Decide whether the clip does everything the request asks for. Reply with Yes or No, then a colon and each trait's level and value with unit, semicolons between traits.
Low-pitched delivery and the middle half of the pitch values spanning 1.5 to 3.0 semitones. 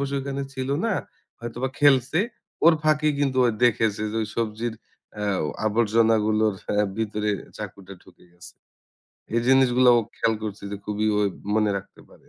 No: low, 115 Hz; average, 3.9 semitones